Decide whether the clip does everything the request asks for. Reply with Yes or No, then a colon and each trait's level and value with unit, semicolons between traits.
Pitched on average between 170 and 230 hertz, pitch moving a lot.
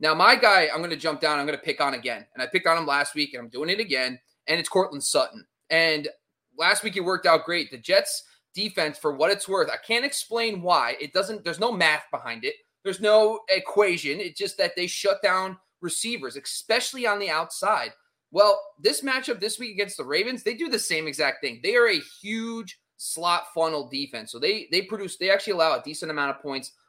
Yes: high, 190 Hz; wide, 6.2 semitones